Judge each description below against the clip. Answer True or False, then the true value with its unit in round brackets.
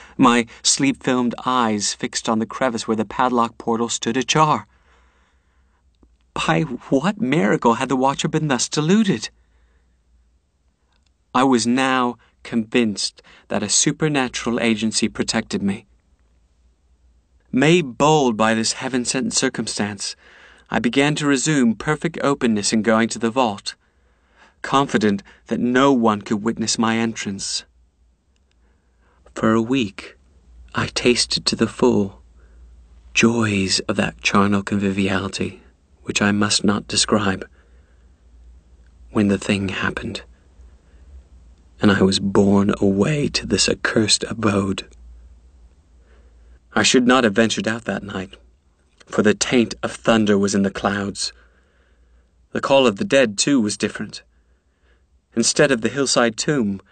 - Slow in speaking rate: True (125 wpm)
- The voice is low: True (100 Hz)